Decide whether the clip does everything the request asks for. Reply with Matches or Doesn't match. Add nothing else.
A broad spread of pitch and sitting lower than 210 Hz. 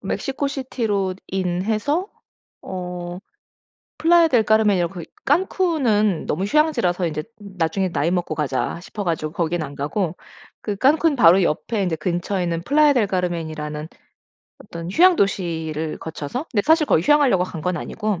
Matches